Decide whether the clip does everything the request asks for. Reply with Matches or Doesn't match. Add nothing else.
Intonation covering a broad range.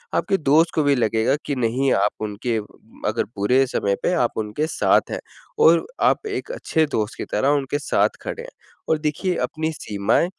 Matches